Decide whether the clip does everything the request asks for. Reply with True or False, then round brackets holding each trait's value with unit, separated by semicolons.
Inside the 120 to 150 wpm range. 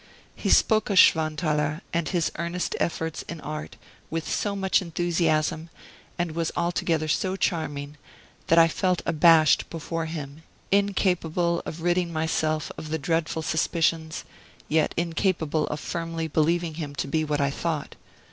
True (145 wpm)